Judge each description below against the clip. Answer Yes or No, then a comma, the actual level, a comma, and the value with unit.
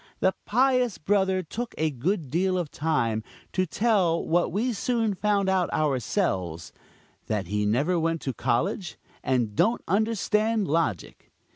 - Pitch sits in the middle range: Yes, medium, 180 Hz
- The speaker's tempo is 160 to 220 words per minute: No, average, 140 wpm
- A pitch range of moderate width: No, wide, 7.7 semitones